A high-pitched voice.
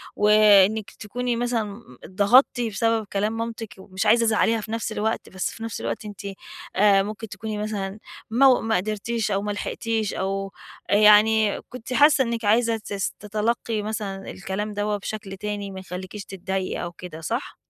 Yes: high, 210 Hz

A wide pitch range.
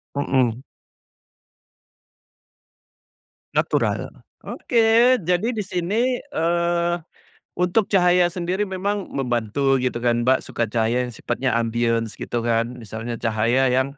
Yes: wide, 7.4 semitones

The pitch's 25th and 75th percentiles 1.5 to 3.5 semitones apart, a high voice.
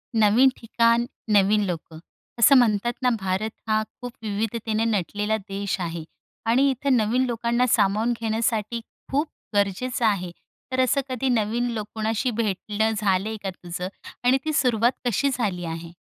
Yes: average, 3.1 semitones; high, 220 Hz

